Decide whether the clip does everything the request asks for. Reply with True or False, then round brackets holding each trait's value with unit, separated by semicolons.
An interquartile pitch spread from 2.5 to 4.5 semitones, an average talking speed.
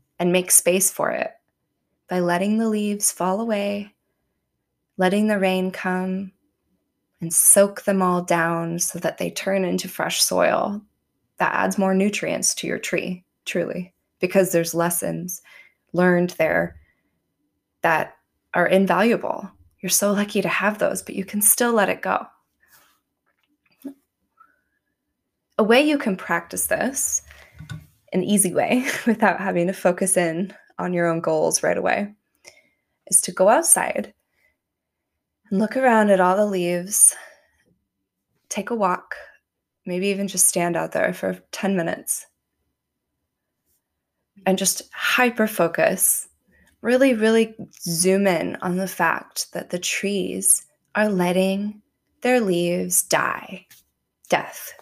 False (2.8 semitones; 130 wpm)